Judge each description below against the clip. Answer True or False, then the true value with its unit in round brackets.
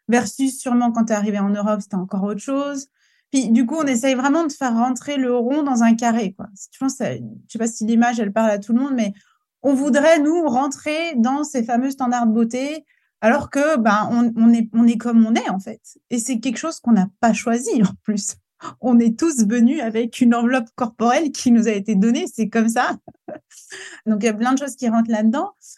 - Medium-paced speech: False (235 wpm)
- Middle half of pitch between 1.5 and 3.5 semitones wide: True (3.1 semitones)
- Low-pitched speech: False (240 Hz)